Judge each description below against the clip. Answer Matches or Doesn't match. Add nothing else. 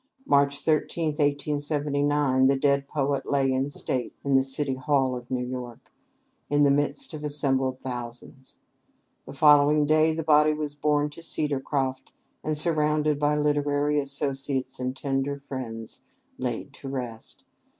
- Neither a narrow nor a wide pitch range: Doesn't match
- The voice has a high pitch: Doesn't match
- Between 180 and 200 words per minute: Doesn't match